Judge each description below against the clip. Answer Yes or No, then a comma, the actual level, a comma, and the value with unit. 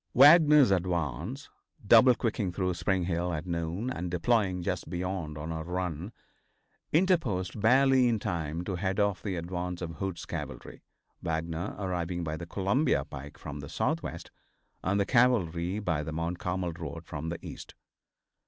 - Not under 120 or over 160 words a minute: Yes, average, 155 wpm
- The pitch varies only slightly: No, average, 3.6 semitones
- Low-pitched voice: Yes, very low, 90 Hz